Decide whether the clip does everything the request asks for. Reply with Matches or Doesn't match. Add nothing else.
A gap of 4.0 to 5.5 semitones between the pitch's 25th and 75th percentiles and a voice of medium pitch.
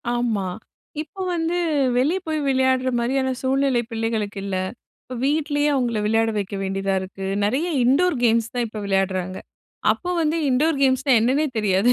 Doesn't match